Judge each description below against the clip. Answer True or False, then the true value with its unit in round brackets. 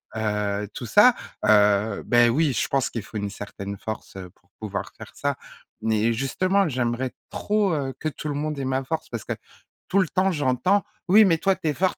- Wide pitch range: True (8.3 semitones)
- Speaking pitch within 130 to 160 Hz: True (135 Hz)